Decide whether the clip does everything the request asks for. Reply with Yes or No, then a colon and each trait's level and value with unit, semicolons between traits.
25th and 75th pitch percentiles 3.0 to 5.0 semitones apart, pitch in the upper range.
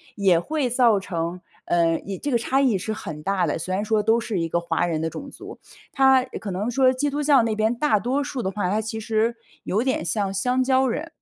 No: wide, 5.6 semitones; high, 220 Hz